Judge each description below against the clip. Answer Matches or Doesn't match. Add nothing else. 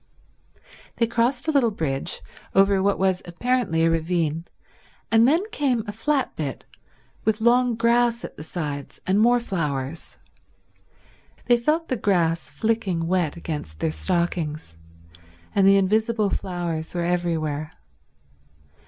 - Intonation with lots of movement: Matches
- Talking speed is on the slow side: Matches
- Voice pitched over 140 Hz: Matches